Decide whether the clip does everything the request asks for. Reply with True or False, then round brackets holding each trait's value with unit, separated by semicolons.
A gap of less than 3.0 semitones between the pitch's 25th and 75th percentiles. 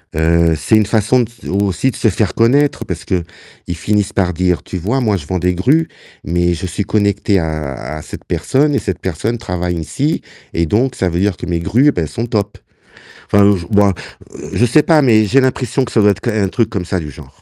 False (4.8 semitones)